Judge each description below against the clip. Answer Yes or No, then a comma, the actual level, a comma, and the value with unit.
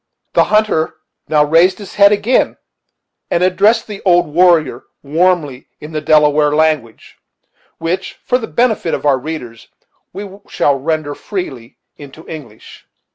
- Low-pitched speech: No, medium, 160 Hz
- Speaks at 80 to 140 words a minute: Yes, slow, 135 wpm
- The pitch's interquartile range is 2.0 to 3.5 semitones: No, average, 4.2 semitones